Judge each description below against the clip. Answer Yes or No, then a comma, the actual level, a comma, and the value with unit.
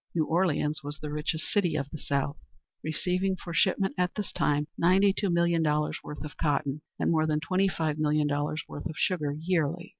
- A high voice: No, medium, 155 Hz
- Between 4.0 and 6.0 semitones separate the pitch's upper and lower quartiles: No, average, 3.1 semitones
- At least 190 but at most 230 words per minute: Yes, average, 200 wpm